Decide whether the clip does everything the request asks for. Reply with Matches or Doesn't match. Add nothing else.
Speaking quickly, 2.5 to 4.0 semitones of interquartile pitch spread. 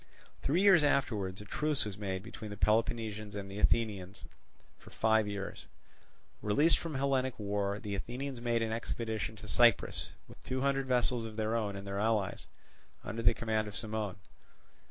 Doesn't match